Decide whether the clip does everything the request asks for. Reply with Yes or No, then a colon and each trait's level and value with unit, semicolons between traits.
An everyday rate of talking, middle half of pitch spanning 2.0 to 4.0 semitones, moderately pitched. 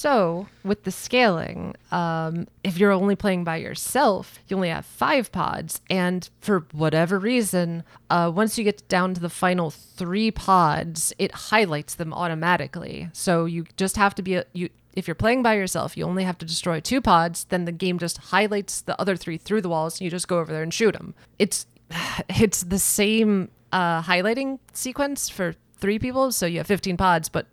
Yes: average, 195 wpm; average, 3.2 semitones; medium, 180 Hz